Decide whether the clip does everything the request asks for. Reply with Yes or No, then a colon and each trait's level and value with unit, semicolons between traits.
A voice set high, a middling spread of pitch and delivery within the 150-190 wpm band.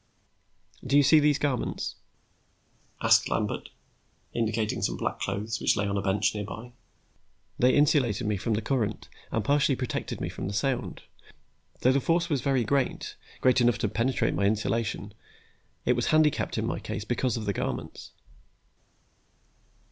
No: low, 120 Hz; average, 4.4 semitones; average, 155 wpm